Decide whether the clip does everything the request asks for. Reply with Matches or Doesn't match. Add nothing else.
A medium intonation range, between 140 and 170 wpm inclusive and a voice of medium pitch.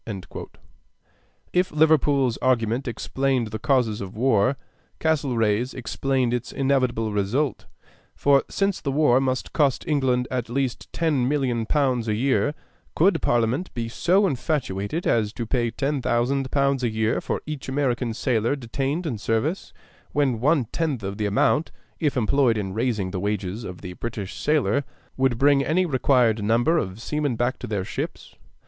Doesn't match